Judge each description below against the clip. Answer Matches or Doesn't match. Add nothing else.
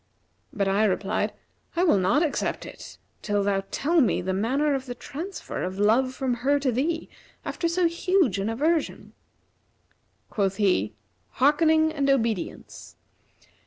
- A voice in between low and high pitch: Doesn't match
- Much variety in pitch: Matches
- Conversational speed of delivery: Matches